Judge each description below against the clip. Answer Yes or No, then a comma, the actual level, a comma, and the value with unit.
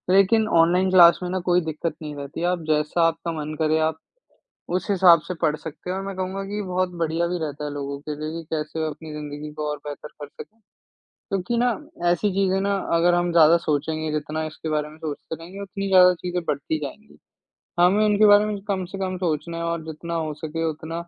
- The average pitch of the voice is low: No, medium, 165 Hz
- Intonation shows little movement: No, average, 3.2 semitones